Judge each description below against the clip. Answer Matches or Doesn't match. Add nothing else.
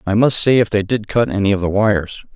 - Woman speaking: Doesn't match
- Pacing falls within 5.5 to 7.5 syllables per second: Matches